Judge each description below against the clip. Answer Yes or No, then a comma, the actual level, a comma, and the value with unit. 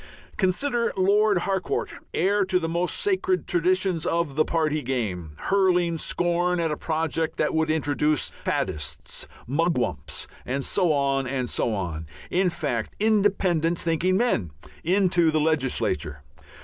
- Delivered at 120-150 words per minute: Yes, slow, 135 wpm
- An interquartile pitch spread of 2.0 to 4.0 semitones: No, average, 5.1 semitones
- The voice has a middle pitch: Yes, medium, 165 Hz